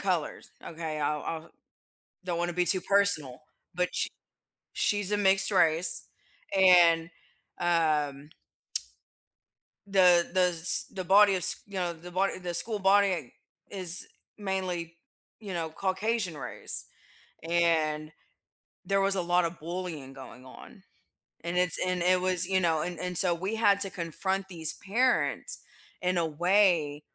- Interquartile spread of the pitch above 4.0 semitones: No, narrow, 2.6 semitones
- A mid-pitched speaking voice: Yes, medium, 180 Hz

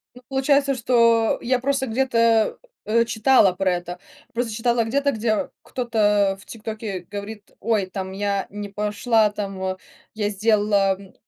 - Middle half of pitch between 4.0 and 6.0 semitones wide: No, average, 2.8 semitones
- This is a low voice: No, high, 215 Hz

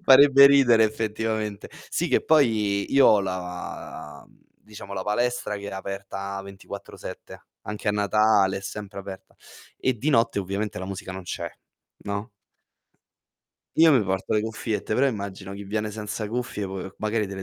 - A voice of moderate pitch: No, low, 105 Hz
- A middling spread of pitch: No, narrow, 2.3 semitones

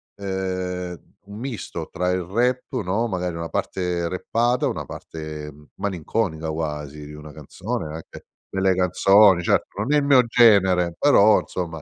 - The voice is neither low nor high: No, very low, 90 Hz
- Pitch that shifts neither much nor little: Yes, average, 4.0 semitones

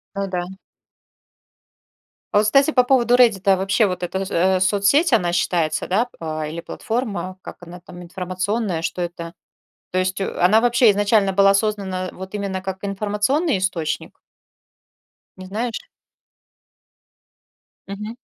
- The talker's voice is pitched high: Yes, high, 195 Hz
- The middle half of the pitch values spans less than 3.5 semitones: Yes, average, 2.9 semitones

